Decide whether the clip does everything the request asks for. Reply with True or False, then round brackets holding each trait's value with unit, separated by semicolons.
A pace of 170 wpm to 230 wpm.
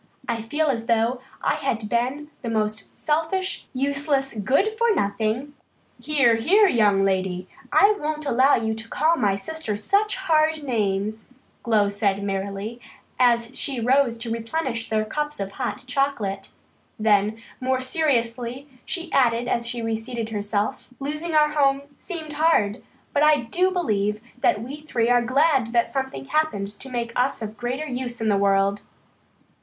False (160 wpm)